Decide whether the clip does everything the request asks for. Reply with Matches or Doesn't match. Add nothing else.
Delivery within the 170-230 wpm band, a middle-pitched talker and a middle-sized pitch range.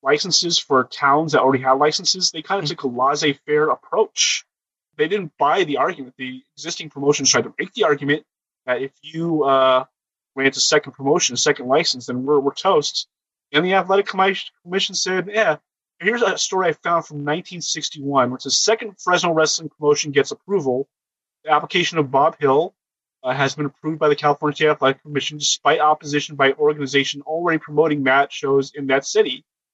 Matches